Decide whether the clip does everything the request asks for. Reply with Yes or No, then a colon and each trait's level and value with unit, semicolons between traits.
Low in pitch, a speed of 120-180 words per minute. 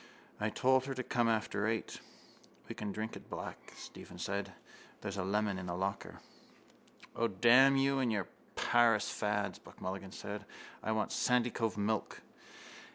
Yes: low, 110 Hz; average, 160 wpm